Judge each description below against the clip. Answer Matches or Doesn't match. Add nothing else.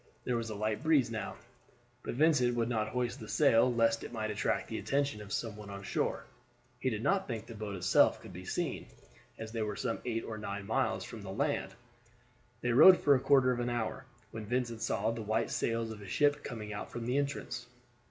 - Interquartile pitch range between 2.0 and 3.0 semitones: Matches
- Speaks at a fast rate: Matches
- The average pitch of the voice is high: Doesn't match